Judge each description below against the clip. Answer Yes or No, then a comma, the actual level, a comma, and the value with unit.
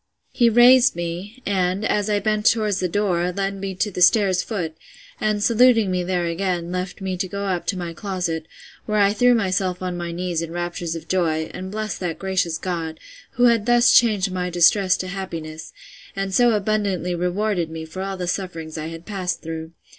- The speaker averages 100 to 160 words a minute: No, average, 200 wpm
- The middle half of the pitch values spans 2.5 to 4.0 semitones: Yes, average, 3.0 semitones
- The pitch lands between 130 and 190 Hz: Yes, medium, 185 Hz